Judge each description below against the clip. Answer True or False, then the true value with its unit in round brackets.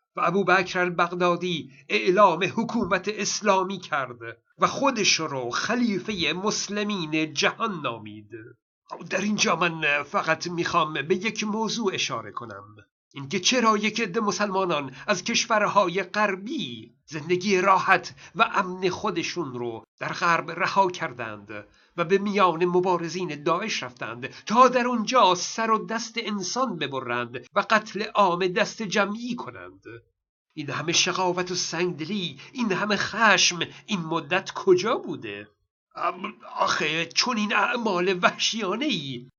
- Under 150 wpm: True (125 wpm)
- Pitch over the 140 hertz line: True (185 Hz)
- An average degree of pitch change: True (4.9 semitones)